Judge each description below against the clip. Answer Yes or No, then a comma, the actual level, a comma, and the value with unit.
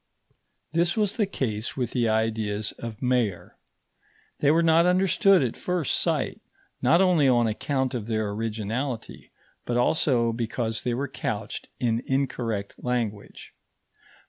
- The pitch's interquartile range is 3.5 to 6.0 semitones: Yes, average, 5.0 semitones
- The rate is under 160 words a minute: Yes, slow, 135 wpm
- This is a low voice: Yes, low, 120 Hz